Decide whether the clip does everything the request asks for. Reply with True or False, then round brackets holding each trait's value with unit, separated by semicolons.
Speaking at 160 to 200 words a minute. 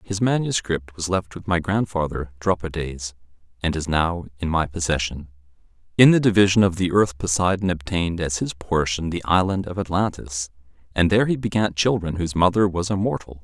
True (170 wpm)